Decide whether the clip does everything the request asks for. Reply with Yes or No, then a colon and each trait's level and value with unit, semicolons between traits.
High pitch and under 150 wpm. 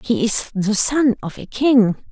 No: high, 225 Hz; average, 200 wpm